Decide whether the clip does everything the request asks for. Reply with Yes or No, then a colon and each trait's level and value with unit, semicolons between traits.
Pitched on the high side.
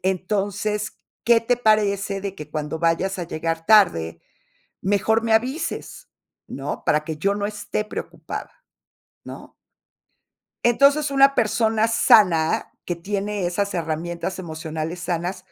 Yes: high, 195 Hz